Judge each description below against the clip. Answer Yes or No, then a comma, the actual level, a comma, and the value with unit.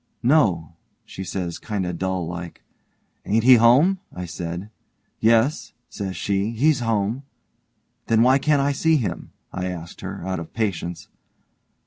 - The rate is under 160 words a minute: Yes, average, 145 wpm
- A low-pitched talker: Yes, low, 105 Hz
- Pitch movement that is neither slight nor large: No, wide, 5.8 semitones